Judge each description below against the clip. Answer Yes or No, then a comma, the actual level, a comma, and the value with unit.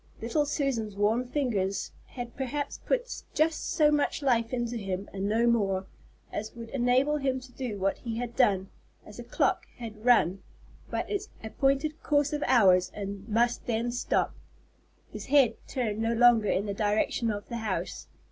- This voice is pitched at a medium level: No, high, 235 Hz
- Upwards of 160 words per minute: Yes, average, 170 wpm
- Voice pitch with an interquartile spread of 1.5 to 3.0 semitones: No, average, 4.3 semitones